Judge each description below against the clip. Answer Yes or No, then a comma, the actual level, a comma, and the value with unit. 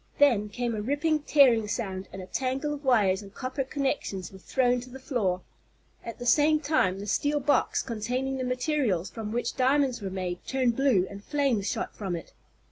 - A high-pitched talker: Yes, high, 245 Hz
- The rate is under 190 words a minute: No, average, 195 wpm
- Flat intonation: No, average, 5.3 semitones